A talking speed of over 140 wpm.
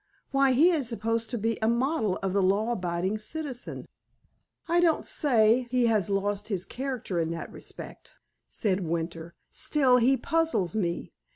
Yes: average, 160 wpm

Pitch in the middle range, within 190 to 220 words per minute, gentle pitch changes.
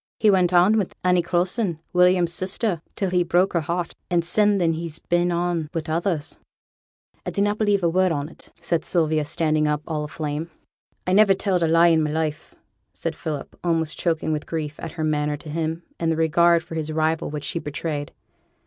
Yes: medium, 165 Hz; average, 200 wpm; narrow, 2.3 semitones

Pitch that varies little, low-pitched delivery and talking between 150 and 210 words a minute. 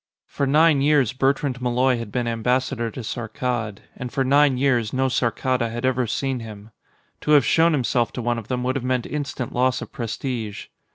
Yes: narrow, 2.3 semitones; low, 125 Hz; average, 190 wpm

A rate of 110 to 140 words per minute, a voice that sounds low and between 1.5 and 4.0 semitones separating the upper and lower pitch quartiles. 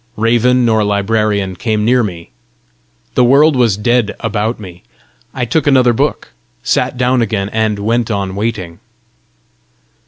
Yes: slow, 135 wpm; low, 110 Hz; average, 3.3 semitones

